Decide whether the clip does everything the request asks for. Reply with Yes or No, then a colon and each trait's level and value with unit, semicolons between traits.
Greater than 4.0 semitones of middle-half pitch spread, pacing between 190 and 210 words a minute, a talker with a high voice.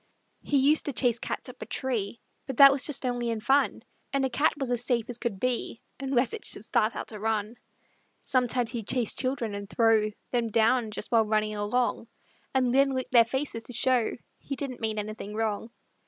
No: average, 2.9 semitones; fast, 205 wpm; high, 240 Hz